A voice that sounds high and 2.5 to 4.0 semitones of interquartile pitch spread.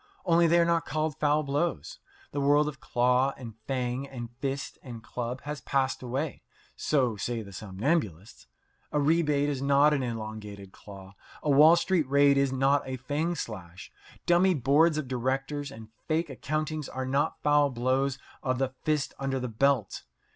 No: low, 135 Hz; average, 3.3 semitones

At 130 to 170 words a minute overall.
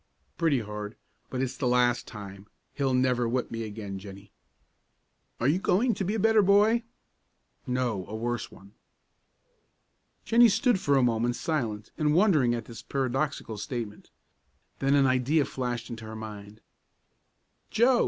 Yes: average, 150 wpm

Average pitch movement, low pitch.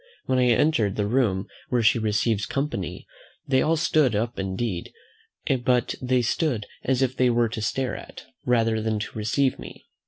Yes: average, 3.2 semitones; low, 120 Hz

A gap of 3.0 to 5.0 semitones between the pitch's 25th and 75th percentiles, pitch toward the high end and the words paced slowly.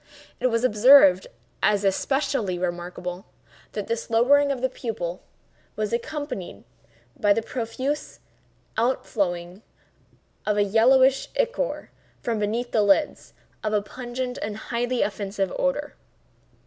Yes: average, 4.3 semitones; high, 225 Hz; slow, 120 wpm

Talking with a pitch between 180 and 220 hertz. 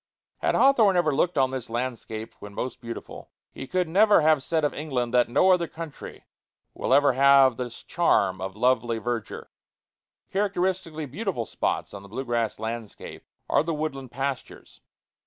No: low, 135 Hz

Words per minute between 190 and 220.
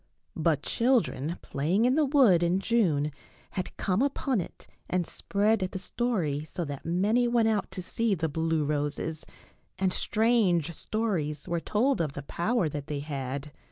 No: average, 160 wpm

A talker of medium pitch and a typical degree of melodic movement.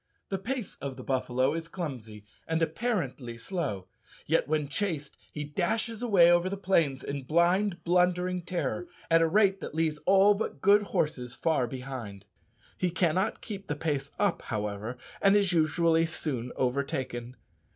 No: medium, 165 Hz; wide, 5.9 semitones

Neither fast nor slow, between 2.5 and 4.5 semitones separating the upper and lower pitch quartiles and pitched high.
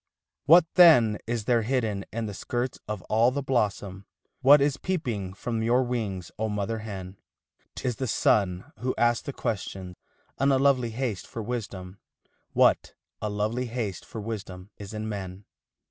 No: average, 165 wpm; average, 3.8 semitones; low, 110 Hz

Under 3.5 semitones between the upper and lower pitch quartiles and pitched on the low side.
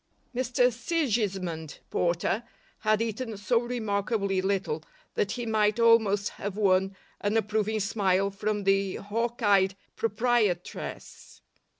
No: average, 2.8 semitones; high, 210 Hz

